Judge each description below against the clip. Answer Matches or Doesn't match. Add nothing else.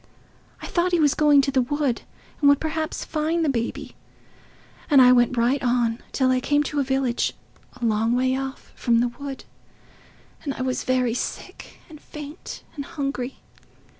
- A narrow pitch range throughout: Doesn't match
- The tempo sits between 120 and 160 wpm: Doesn't match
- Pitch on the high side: Matches